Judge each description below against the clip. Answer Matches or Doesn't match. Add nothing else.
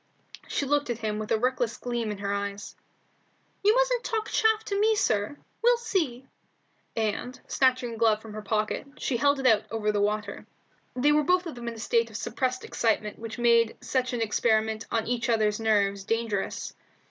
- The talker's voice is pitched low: Doesn't match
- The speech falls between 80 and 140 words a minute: Doesn't match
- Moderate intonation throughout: Matches